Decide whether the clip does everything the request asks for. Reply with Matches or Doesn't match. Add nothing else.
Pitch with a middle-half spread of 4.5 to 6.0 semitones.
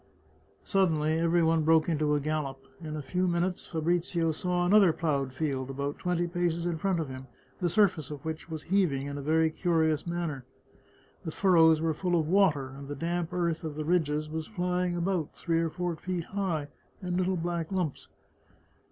Doesn't match